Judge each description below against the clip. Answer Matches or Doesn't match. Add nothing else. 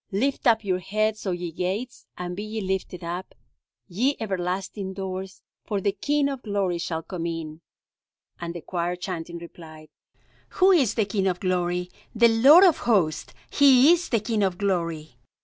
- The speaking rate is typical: Matches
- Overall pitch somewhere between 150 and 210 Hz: Matches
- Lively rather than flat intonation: Doesn't match